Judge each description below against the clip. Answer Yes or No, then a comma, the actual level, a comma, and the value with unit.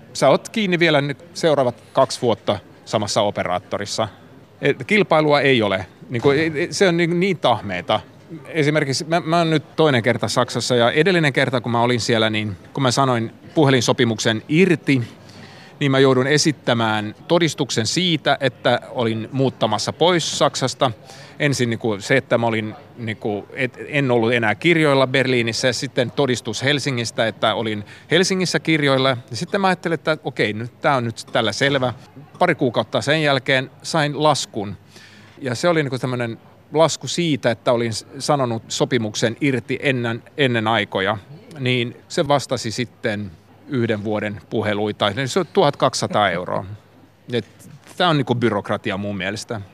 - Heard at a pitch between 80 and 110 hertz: No, low, 130 Hz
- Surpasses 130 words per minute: Yes, average, 150 wpm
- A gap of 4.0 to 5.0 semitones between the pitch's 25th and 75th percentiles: Yes, average, 4.6 semitones